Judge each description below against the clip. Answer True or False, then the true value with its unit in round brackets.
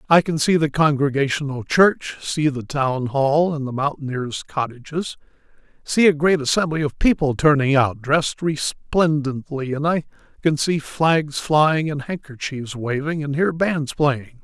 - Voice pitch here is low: False (145 Hz)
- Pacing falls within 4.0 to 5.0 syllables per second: True (4.2 syllables/s)